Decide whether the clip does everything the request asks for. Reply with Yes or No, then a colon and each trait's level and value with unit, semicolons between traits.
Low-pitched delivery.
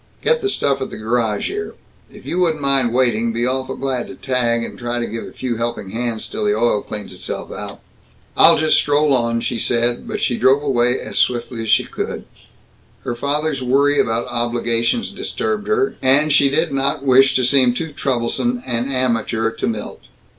Yes: low, 125 Hz